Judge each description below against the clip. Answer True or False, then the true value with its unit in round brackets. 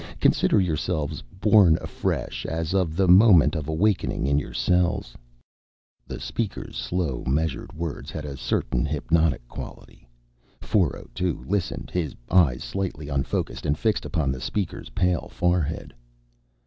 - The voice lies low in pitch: True (80 Hz)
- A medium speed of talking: False (130 wpm)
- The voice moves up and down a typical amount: True (4.0 semitones)